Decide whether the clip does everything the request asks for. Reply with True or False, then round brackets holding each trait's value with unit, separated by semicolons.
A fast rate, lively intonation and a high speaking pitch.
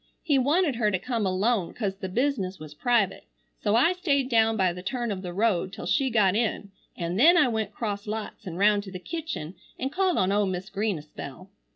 False (220 wpm; 4.8 semitones; 210 Hz)